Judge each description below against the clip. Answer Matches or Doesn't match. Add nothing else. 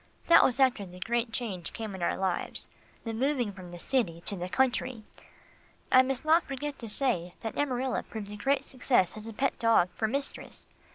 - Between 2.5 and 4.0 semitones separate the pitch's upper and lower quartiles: Doesn't match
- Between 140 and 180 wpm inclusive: Doesn't match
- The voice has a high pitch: Matches